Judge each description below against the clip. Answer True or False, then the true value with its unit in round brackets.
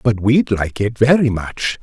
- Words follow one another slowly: False (200 wpm)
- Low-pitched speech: True (115 Hz)